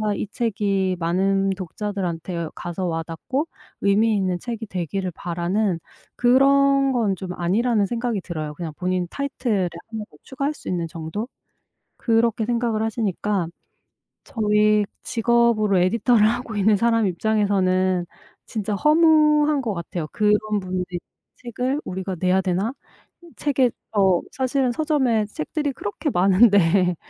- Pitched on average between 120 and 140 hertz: No, high, 210 Hz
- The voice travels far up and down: No, average, 4.4 semitones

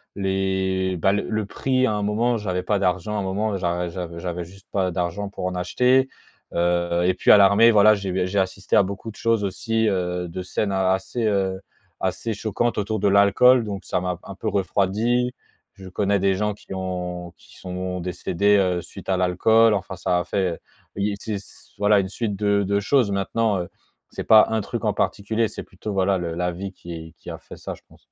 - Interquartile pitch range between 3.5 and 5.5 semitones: No, narrow, 2.4 semitones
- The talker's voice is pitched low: Yes, very low, 95 Hz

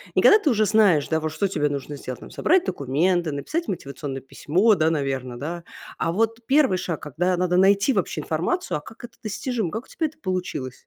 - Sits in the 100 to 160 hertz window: No, medium, 180 Hz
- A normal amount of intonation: No, wide, 7.0 semitones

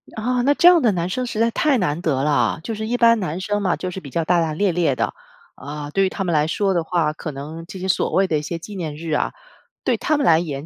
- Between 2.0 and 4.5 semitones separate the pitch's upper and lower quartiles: No, wide, 5.4 semitones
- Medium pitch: Yes, medium, 175 Hz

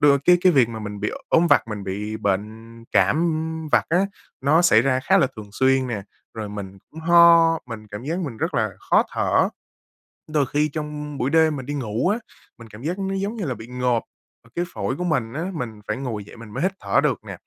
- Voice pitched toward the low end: Yes, low, 130 Hz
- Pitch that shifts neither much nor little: No, wide, 6.5 semitones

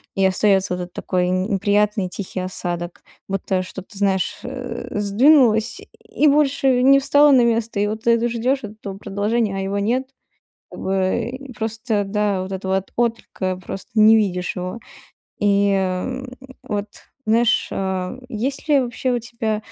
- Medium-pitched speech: No, high, 210 Hz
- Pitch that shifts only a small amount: No, average, 3.8 semitones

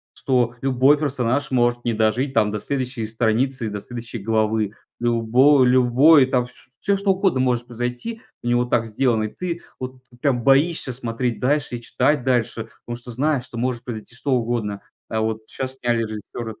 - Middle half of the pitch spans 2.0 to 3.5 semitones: Yes, narrow, 2.6 semitones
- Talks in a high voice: No, low, 120 Hz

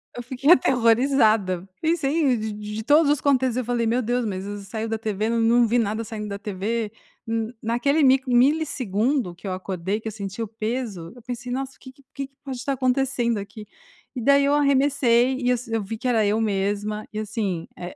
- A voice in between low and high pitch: No, high, 230 Hz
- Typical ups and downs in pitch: Yes, average, 3.7 semitones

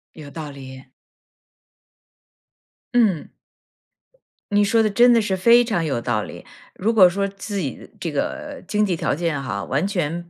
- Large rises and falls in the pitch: Yes, wide, 6.2 semitones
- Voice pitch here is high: No, medium, 180 Hz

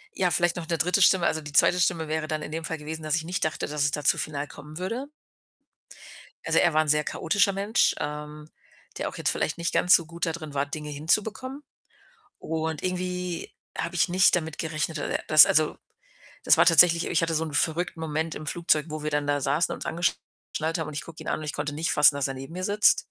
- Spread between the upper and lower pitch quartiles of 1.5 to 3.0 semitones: Yes, narrow, 2.6 semitones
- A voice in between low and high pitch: Yes, medium, 160 Hz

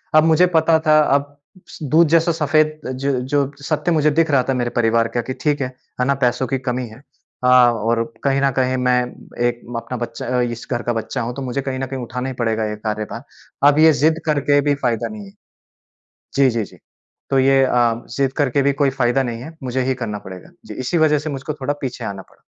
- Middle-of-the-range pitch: No, low, 130 Hz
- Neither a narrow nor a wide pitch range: Yes, average, 3.3 semitones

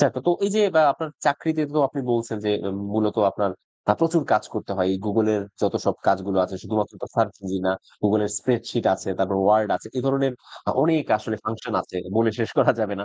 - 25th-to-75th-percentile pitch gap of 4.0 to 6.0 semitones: Yes, average, 4.8 semitones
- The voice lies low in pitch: Yes, low, 110 Hz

